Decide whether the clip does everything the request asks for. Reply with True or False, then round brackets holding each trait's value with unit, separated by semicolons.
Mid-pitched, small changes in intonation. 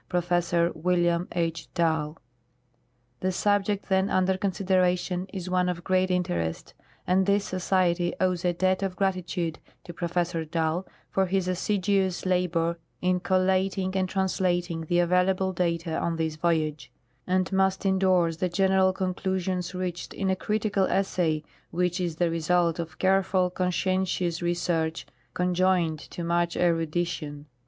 True (180 Hz; 1.8 semitones)